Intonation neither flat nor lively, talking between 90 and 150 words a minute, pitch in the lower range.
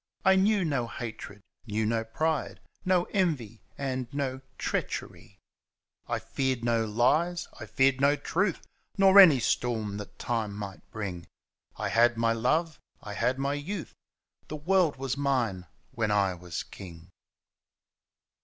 No: wide, 5.9 semitones; average, 140 wpm; low, 125 Hz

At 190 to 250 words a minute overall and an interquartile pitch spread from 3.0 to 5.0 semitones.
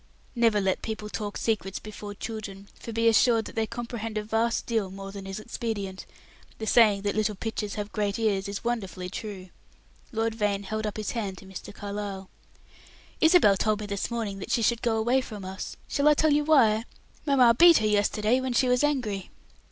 No: average, 200 wpm; narrow, 2.6 semitones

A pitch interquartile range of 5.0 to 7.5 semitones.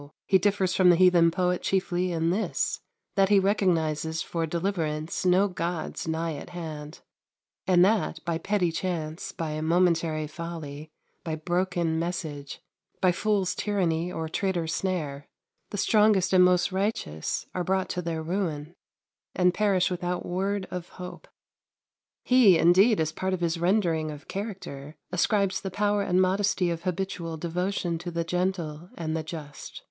No: average, 2.7 semitones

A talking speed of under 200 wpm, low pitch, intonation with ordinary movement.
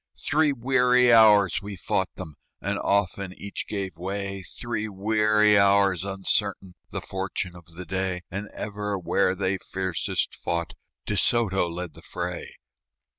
No: average, 140 wpm; low, 100 Hz; narrow, 2.2 semitones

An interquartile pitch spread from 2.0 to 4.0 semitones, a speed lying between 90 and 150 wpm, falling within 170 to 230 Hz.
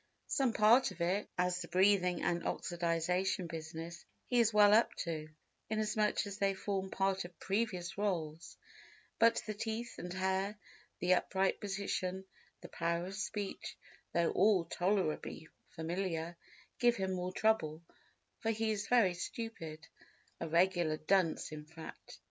Yes: average, 3.4 semitones; slow, 135 wpm; high, 190 Hz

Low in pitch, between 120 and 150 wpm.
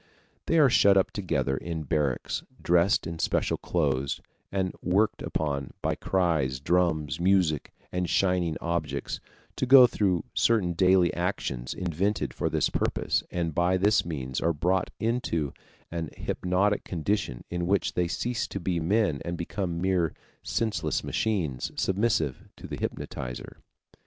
Yes: very low, 90 Hz; average, 140 wpm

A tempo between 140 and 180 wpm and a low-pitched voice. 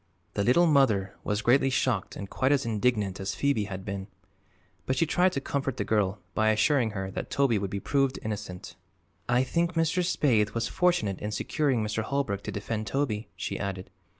No: average, 190 wpm; low, 110 Hz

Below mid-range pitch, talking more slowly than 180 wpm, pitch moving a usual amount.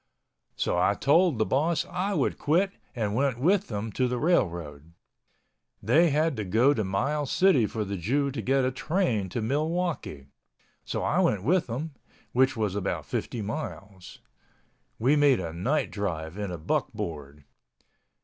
No: low, 125 Hz; average, 160 wpm; wide, 7.2 semitones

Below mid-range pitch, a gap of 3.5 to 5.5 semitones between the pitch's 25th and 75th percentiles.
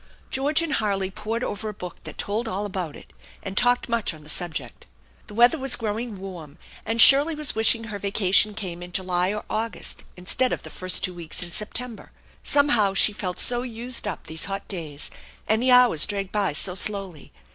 No: high, 205 Hz; average, 4.3 semitones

